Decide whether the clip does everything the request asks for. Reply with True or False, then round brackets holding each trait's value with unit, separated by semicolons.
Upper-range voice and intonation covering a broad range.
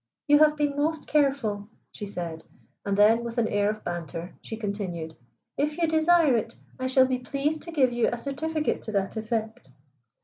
True (235 Hz; 6.3 semitones)